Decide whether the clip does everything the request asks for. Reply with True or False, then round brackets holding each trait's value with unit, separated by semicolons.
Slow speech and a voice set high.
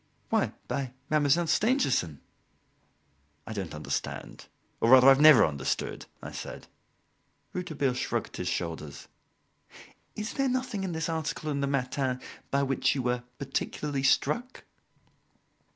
False (130 wpm; 140 Hz)